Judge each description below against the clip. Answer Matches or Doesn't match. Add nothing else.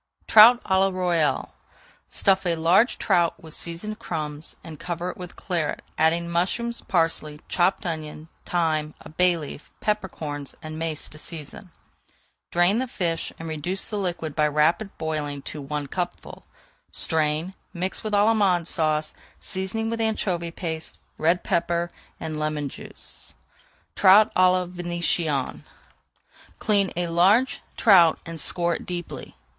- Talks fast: Doesn't match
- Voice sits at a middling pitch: Matches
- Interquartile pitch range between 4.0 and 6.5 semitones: Doesn't match